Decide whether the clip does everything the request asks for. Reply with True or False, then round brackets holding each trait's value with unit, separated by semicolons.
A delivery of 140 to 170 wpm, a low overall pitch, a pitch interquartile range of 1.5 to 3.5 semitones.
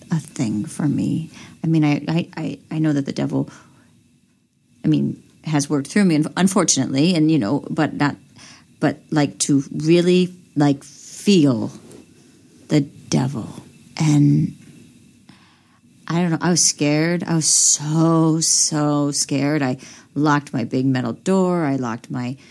False (145 wpm; 150 Hz; 2.7 semitones)